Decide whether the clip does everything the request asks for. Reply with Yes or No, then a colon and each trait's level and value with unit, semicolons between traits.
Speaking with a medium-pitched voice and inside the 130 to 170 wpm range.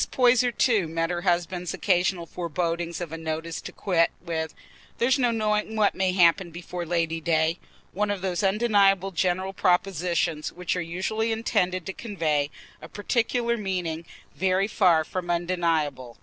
Yes: medium, 180 Hz; average, 150 wpm